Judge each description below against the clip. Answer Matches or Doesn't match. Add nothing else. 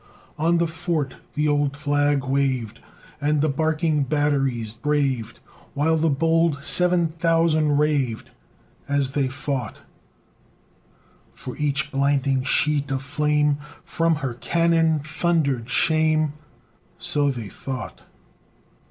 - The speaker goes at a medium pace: Doesn't match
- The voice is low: Doesn't match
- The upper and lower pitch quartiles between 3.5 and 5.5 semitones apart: Doesn't match